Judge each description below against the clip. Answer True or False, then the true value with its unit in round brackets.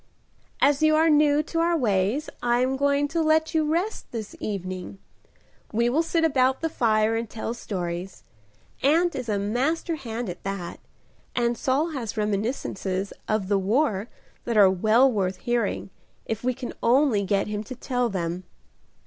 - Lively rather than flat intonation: True (6.1 semitones)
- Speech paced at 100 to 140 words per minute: False (165 wpm)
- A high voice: True (240 Hz)